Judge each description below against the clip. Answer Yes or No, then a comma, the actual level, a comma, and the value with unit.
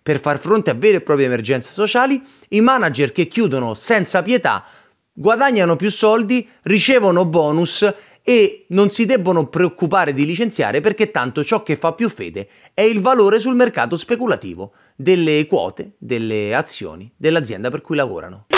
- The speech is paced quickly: No, average, 155 wpm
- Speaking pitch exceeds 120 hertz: Yes, medium, 185 Hz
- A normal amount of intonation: No, wide, 6.6 semitones